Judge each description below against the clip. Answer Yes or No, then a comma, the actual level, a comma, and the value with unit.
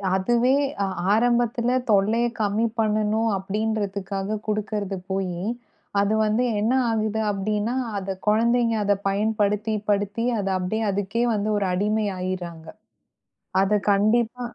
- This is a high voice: Yes, high, 210 Hz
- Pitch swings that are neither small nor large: No, narrow, 2.0 semitones